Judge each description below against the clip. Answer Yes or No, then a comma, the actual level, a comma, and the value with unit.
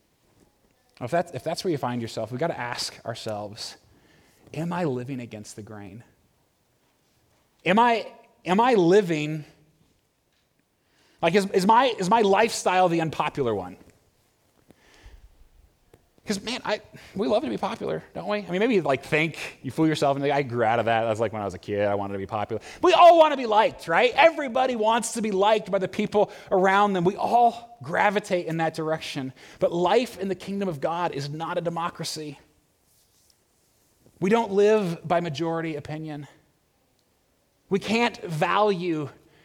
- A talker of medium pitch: Yes, medium, 170 Hz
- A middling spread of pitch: No, wide, 6.6 semitones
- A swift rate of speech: No, average, 175 wpm